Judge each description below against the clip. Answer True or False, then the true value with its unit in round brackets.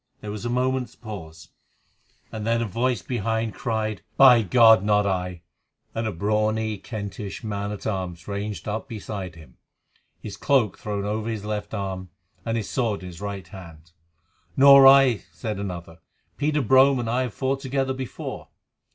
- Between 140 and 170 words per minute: True (160 wpm)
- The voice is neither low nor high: False (110 Hz)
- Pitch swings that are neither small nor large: True (3.4 semitones)